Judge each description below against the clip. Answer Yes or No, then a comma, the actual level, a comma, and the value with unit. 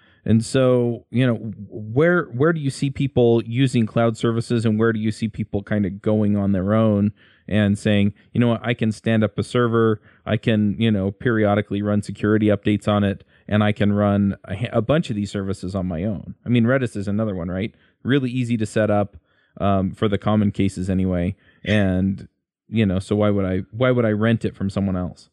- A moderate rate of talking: No, fast, 220 wpm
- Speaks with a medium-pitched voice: No, low, 105 Hz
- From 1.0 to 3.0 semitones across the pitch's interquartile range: Yes, narrow, 2.5 semitones